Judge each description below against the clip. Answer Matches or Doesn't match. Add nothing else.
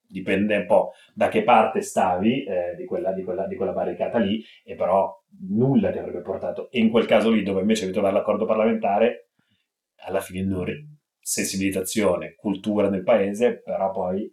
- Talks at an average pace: Doesn't match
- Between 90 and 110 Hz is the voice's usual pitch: Matches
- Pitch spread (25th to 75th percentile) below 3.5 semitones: Matches